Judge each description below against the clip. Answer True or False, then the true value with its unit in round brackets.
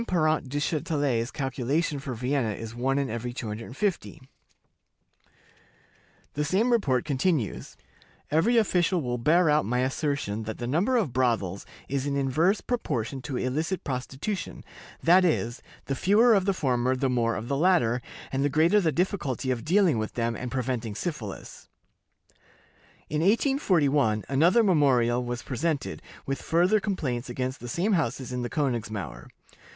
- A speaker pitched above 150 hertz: False (140 Hz)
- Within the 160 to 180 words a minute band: False (145 wpm)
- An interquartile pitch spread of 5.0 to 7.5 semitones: True (5.6 semitones)